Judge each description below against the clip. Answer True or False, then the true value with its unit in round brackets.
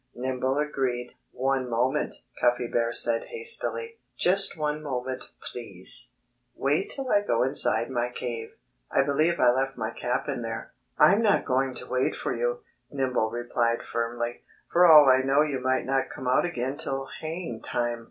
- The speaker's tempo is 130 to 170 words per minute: True (165 wpm)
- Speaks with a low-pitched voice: True (130 Hz)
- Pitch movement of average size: True (3.6 semitones)